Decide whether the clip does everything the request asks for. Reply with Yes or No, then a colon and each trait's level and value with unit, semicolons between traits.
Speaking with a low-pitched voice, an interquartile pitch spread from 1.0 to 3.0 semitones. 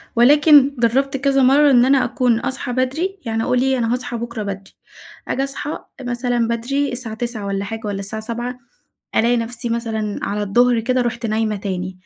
No: high, 240 Hz; average, 2.7 semitones